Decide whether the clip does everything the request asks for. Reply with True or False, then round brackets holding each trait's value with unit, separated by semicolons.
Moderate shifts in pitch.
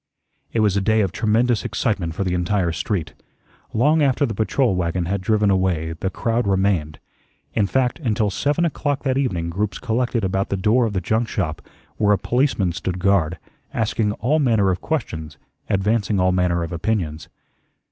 True (4.1 semitones)